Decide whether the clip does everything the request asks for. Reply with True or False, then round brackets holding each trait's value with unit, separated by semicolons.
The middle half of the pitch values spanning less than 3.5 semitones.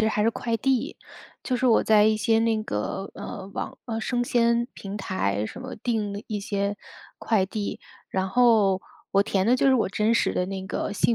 True (2.9 semitones)